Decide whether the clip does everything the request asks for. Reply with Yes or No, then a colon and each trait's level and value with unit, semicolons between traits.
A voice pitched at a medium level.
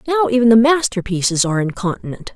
No: high, 220 Hz